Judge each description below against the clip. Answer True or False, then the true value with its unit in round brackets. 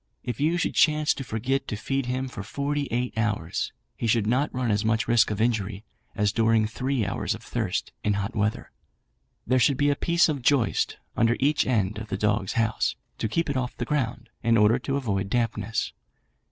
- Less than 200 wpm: False (205 wpm)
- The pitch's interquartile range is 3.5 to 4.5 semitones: True (3.9 semitones)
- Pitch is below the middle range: True (115 Hz)